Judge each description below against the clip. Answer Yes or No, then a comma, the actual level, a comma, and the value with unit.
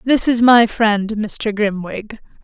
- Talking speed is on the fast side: No, average, 150 wpm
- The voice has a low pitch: No, high, 220 Hz